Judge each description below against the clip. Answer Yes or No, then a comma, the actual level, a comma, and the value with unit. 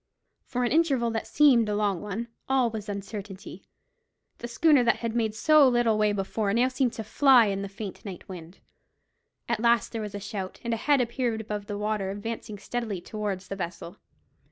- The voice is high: Yes, high, 220 Hz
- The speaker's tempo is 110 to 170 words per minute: No, average, 195 wpm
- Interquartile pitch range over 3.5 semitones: No, average, 3.0 semitones